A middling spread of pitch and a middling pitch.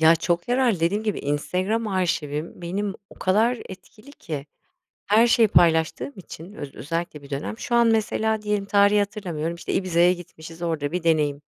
Yes: average, 4.5 semitones; medium, 180 Hz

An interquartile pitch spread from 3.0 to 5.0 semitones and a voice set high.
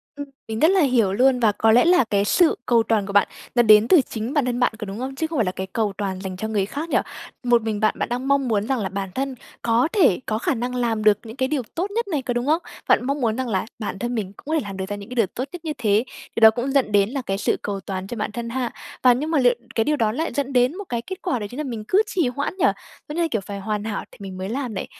Yes: average, 4.4 semitones; high, 240 Hz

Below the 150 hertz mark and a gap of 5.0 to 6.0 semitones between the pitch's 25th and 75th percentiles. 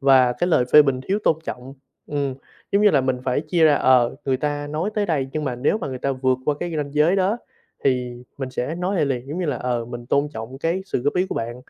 No: medium, 140 Hz; average, 3.8 semitones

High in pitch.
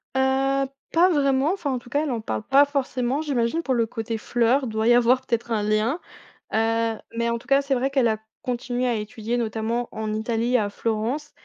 Yes: high, 240 Hz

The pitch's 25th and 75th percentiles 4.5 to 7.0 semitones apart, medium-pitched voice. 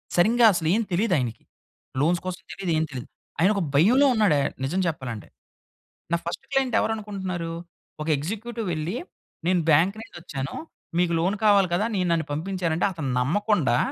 Yes: average, 4.8 semitones; medium, 180 Hz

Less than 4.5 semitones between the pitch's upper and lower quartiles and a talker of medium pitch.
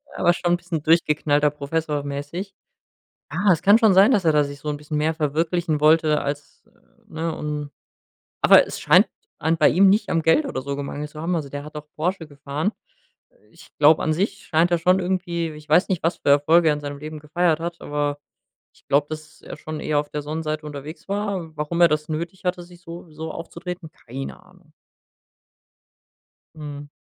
Yes: average, 2.7 semitones; medium, 155 Hz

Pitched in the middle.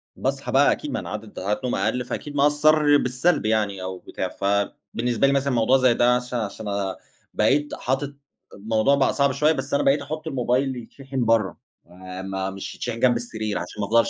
No: low, 125 Hz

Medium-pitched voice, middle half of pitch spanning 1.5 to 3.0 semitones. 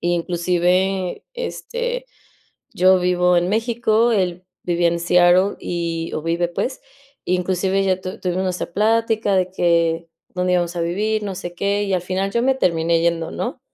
Yes: medium, 180 Hz; narrow, 2.5 semitones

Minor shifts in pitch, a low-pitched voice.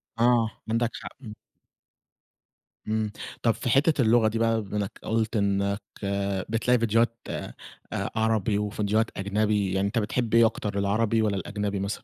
Yes: narrow, 2.0 semitones; low, 110 Hz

